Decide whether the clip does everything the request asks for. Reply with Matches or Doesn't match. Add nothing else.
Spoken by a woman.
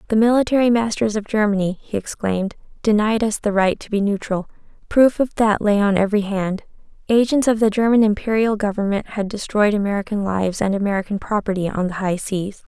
Matches